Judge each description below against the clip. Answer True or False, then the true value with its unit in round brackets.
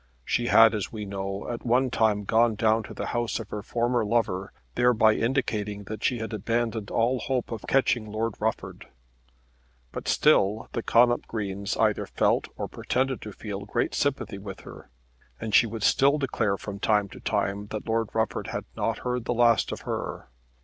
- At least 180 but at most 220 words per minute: True (185 wpm)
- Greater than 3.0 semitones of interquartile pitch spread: False (2.5 semitones)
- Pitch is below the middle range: True (110 Hz)